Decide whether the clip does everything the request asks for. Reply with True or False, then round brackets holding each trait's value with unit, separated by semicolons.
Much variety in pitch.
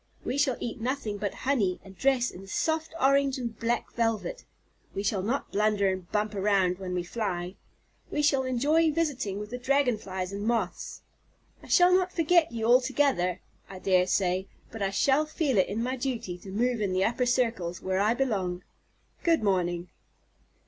True (5.8 semitones)